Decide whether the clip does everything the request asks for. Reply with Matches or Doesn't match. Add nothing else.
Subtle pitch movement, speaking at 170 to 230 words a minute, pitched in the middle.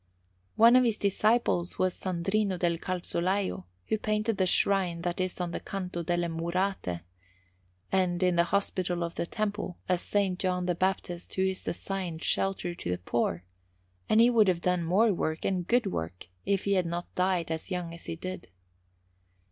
Matches